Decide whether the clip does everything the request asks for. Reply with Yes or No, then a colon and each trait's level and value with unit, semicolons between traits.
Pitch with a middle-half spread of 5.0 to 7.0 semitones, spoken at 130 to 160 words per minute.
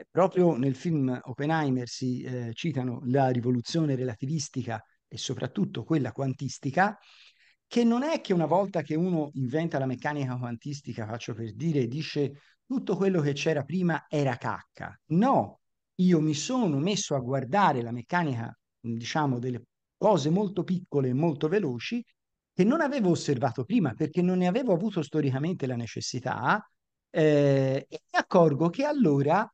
Yes: wide, 5.5 semitones; average, 150 wpm